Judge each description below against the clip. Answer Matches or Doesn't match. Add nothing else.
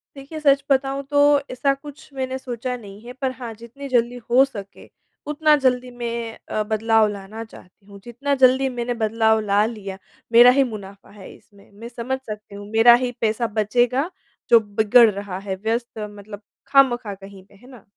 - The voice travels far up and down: Doesn't match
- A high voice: Matches